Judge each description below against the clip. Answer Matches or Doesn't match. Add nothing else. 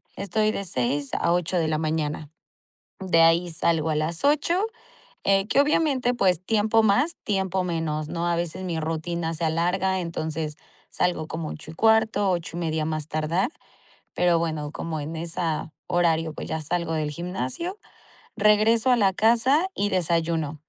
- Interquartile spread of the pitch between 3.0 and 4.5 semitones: Matches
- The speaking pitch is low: Doesn't match